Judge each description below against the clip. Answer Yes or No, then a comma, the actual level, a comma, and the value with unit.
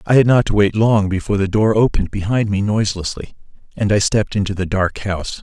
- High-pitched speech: No, low, 105 Hz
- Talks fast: Yes, fast, 220 wpm